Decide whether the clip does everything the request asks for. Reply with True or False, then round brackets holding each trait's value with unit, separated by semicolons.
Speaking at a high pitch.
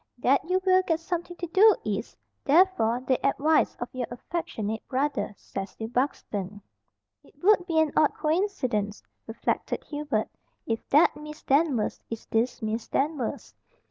True (275 Hz)